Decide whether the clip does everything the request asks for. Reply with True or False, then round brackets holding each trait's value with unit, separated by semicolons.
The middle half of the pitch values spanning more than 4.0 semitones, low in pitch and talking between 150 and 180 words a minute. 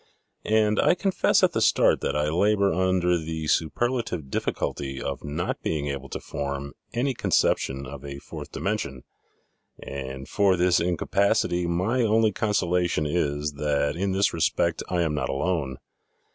True (5.4 semitones; 85 Hz; 155 wpm)